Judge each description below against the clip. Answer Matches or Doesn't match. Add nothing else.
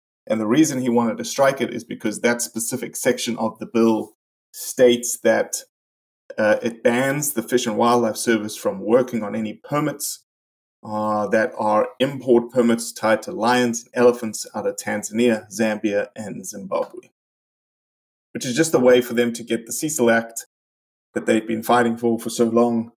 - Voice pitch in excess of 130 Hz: Doesn't match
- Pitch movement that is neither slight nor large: Doesn't match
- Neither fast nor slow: Matches